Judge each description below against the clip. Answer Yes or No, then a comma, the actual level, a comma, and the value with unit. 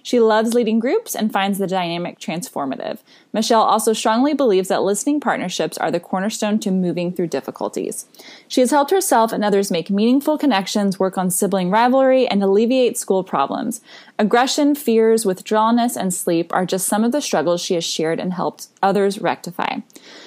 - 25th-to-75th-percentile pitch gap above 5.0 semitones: No, average, 4.5 semitones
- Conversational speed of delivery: Yes, average, 170 wpm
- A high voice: Yes, high, 215 Hz